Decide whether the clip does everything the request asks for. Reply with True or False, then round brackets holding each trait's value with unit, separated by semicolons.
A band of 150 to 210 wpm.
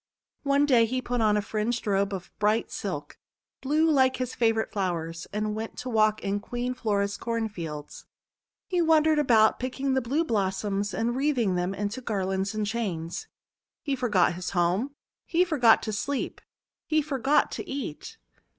True (165 wpm)